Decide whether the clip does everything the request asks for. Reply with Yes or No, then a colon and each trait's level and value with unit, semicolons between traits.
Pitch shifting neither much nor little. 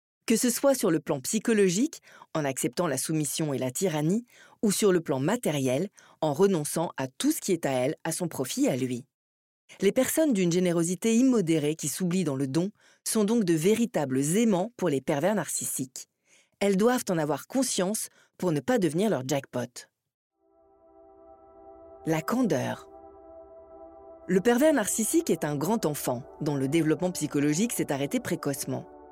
No: wide, 7.2 semitones